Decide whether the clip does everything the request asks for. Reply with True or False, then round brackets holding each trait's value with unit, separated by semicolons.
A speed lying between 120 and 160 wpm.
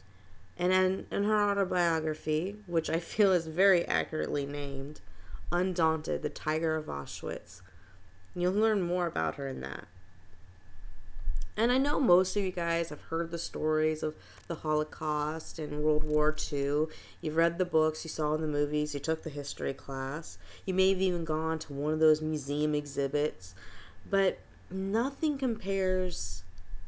True (155 wpm)